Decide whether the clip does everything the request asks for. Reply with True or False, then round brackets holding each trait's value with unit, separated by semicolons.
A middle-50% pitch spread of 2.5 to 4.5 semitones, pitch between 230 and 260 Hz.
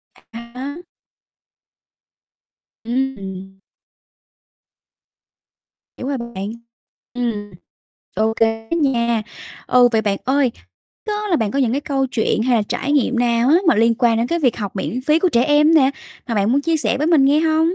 True (4.2 semitones; 250 Hz)